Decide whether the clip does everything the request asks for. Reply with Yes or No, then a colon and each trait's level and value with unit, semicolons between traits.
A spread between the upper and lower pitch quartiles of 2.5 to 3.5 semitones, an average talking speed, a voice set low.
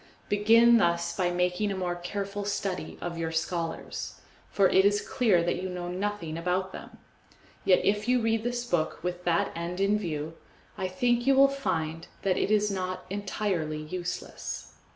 No: average, 3.0 semitones; average, 175 wpm; medium, 185 Hz